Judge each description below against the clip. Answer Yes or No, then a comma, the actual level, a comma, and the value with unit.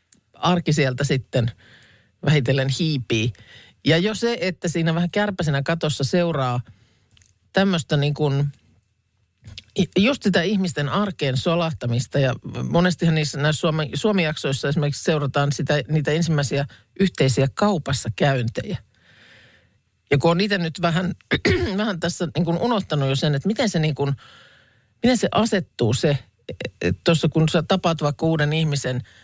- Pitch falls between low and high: Yes, medium, 150 Hz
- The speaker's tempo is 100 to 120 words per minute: No, average, 130 wpm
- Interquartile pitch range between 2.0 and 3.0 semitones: No, average, 4.7 semitones